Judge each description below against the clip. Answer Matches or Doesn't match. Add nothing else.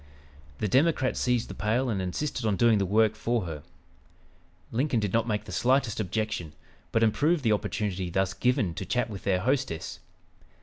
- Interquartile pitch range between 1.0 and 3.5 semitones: Doesn't match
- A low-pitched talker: Matches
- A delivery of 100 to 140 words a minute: Doesn't match